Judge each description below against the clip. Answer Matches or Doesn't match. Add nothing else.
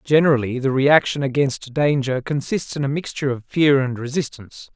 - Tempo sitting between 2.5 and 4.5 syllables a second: Doesn't match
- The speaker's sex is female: Doesn't match